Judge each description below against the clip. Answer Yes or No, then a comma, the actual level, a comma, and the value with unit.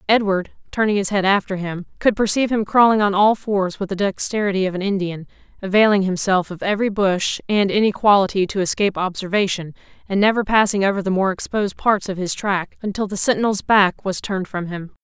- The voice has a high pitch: Yes, high, 195 Hz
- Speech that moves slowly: No, average, 190 wpm